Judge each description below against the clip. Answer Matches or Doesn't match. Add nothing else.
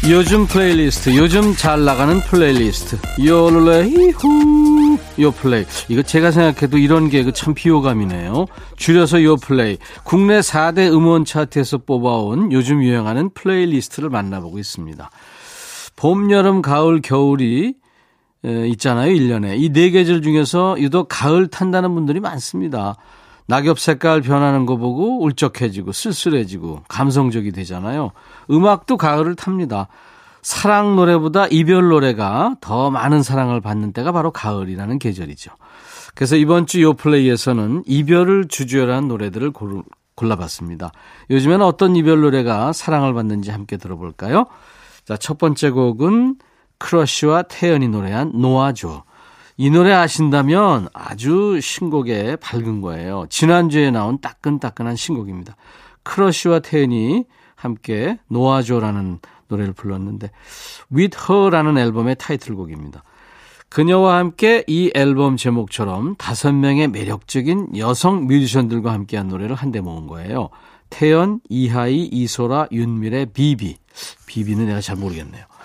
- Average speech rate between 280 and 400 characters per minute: Matches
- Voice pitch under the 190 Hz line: Matches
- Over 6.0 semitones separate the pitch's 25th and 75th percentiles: Matches